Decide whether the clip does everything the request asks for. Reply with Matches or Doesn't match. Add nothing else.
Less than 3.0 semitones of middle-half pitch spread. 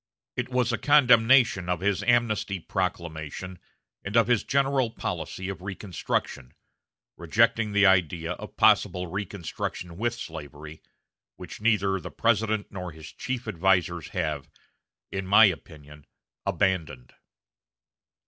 Doesn't match